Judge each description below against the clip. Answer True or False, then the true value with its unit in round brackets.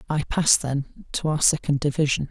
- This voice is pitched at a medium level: True (145 Hz)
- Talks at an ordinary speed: True (180 wpm)